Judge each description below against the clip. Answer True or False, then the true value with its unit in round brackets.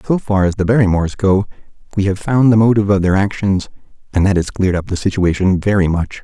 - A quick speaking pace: True (220 wpm)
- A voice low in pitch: True (100 Hz)